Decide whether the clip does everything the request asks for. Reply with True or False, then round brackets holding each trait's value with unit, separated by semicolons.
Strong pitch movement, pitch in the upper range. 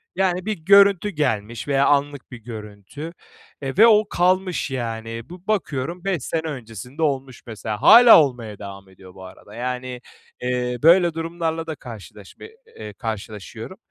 False (7.2 semitones; 135 Hz)